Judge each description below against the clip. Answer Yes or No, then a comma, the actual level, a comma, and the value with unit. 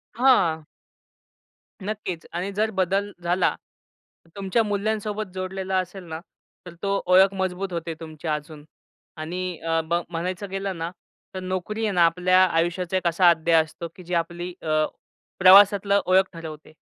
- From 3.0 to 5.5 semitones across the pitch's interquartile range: No, narrow, 2.6 semitones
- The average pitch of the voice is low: No, medium, 185 Hz